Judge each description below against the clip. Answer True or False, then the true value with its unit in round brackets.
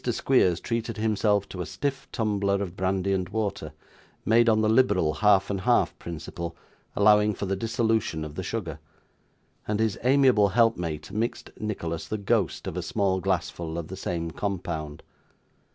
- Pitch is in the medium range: False (100 Hz)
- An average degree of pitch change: True (4.0 semitones)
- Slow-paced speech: False (160 wpm)